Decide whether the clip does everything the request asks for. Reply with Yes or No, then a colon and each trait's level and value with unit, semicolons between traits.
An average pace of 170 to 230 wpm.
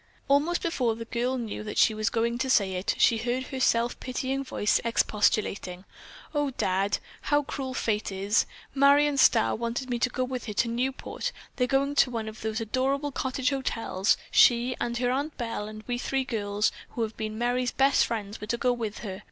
Yes: average, 200 wpm